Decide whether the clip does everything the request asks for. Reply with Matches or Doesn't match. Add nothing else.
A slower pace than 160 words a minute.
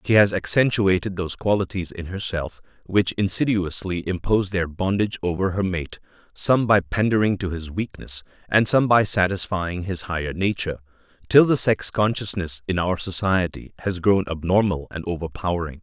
Matches